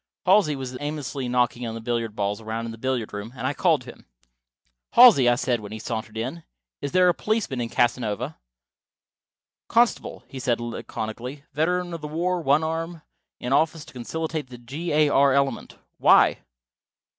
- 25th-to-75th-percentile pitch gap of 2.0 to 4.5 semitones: No, average, 5.1 semitones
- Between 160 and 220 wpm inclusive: Yes, average, 175 wpm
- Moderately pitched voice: No, low, 130 Hz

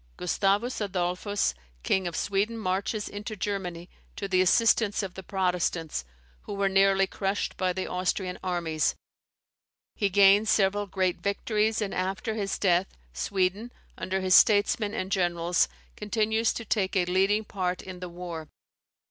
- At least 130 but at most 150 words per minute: Yes, average, 145 wpm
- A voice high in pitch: Yes, high, 195 Hz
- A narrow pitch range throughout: Yes, narrow, 2.1 semitones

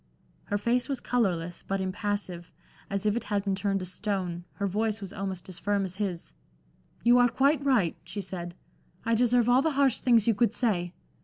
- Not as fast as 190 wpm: No, average, 200 wpm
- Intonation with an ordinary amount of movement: Yes, average, 4.1 semitones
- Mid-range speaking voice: No, high, 205 Hz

